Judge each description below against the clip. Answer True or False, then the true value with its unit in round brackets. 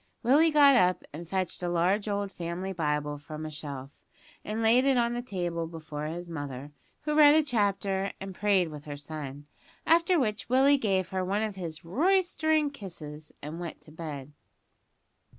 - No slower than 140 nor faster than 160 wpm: False (175 wpm)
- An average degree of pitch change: False (7.3 semitones)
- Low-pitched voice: False (185 Hz)